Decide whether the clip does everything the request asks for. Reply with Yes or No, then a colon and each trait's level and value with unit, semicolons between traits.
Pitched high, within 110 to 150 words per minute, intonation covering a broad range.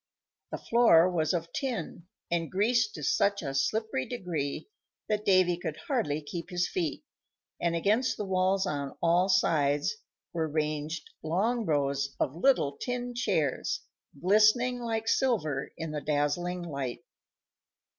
No: medium, 175 Hz; slow, 135 wpm; wide, 6.0 semitones